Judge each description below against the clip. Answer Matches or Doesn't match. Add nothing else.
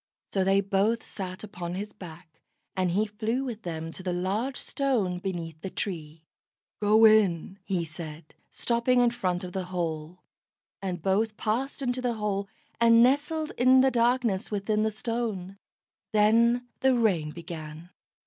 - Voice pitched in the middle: Doesn't match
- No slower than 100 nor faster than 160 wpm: Matches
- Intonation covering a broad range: Doesn't match